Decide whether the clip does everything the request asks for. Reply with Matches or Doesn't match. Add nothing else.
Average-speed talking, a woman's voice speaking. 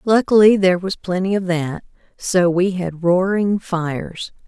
Matches